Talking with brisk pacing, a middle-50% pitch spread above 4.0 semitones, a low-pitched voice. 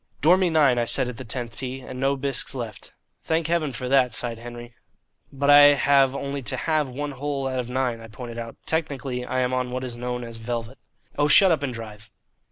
No: fast, 220 wpm; average, 2.9 semitones; low, 130 Hz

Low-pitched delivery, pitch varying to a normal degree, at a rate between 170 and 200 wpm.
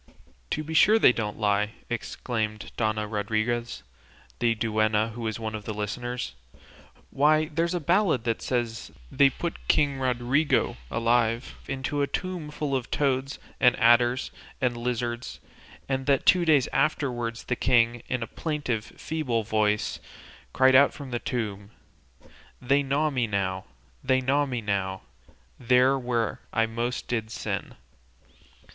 No: low, 120 Hz; average, 3.5 semitones; average, 145 wpm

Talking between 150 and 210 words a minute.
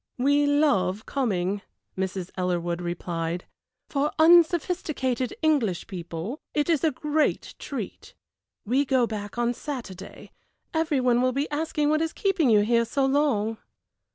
No: slow, 135 wpm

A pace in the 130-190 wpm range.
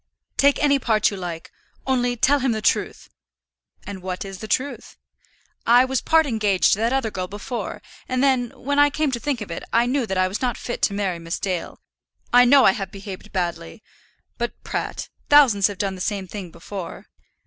No: fast, 205 wpm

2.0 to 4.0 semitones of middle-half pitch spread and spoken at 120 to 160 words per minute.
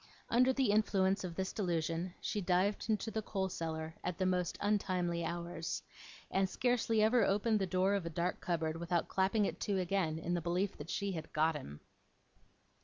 No: average, 3.1 semitones; average, 185 wpm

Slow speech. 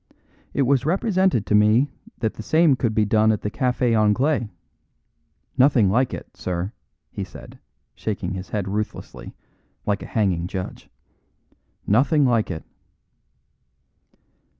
Yes: slow, 130 wpm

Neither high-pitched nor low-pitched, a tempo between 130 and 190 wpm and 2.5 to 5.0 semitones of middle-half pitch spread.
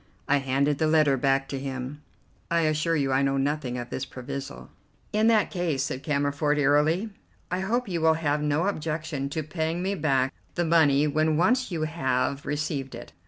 Yes: medium, 150 Hz; average, 185 wpm; average, 3.0 semitones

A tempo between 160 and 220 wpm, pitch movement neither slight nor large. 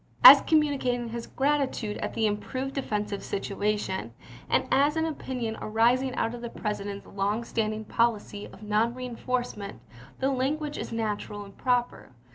No: average, 150 wpm; average, 3.6 semitones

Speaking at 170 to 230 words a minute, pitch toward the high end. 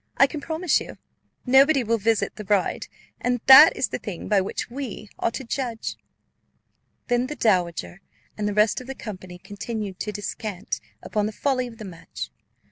Yes: average, 180 wpm; high, 225 Hz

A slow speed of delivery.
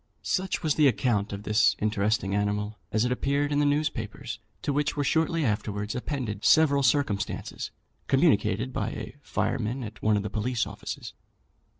No: average, 165 wpm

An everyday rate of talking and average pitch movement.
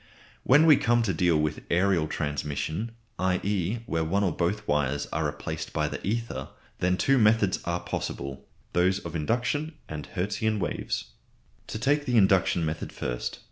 No: average, 160 wpm; wide, 6.0 semitones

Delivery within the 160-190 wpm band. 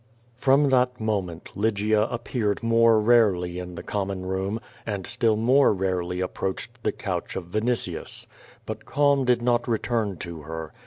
No: average, 150 wpm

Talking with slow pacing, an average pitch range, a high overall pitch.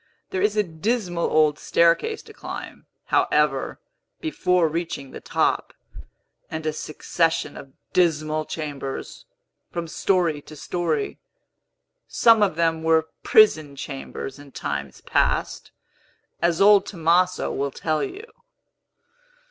No: slow, 115 wpm; average, 3.3 semitones; medium, 165 Hz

